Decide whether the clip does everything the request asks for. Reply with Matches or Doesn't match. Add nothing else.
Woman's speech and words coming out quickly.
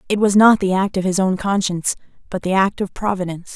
Matches